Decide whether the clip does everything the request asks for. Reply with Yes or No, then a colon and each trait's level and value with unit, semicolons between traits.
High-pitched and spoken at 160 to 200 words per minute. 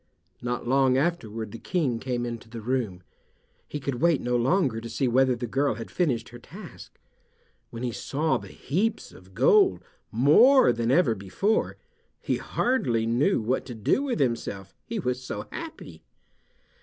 No: low, 125 Hz; average, 165 wpm